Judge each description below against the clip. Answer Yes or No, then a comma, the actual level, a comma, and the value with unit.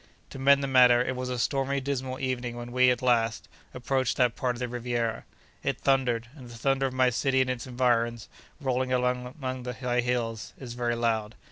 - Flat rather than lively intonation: Yes, narrow, 1.4 semitones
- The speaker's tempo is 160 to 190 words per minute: No, fast, 205 wpm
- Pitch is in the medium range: No, low, 125 Hz